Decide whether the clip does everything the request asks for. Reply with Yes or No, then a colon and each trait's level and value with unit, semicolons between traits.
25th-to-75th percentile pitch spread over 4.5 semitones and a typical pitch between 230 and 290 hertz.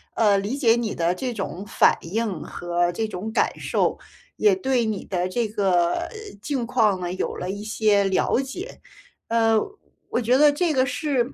No: average, 4.9 semitones; high, 220 Hz